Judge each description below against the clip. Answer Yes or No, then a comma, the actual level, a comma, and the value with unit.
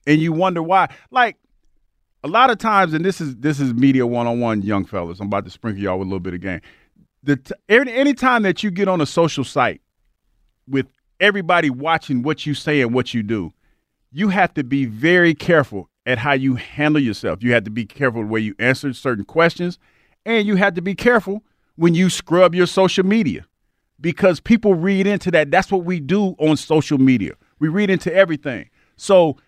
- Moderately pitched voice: Yes, medium, 155 Hz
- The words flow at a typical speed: No, fast, 210 wpm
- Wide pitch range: Yes, wide, 7.0 semitones